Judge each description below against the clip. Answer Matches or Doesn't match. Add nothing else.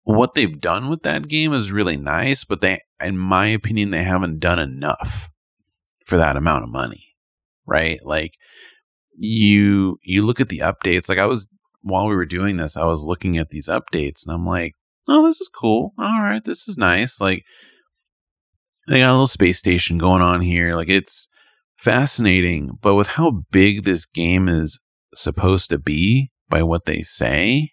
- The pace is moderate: Matches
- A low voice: Matches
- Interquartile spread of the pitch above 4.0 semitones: Matches